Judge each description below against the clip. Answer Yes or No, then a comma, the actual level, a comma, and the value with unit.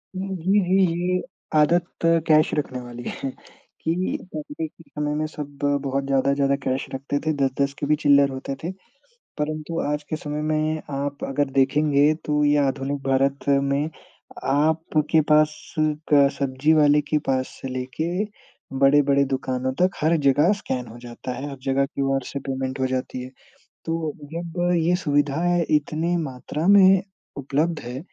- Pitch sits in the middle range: Yes, medium, 145 Hz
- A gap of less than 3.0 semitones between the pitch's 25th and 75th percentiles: Yes, narrow, 2.4 semitones